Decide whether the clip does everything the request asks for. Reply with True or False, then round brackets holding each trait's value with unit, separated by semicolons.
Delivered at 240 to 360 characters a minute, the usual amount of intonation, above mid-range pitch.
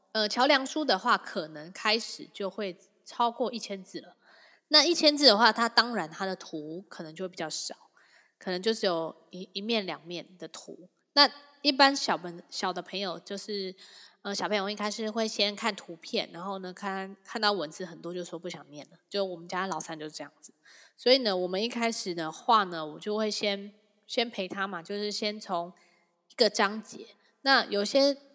True (275 characters per minute; 4.0 semitones; 200 Hz)